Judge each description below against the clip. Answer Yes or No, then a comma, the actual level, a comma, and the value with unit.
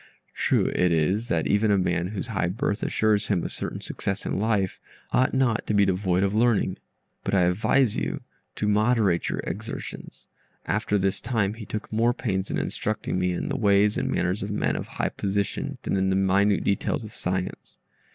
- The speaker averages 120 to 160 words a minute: No, average, 195 wpm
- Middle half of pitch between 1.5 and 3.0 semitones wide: Yes, narrow, 2.6 semitones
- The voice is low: Yes, low, 100 Hz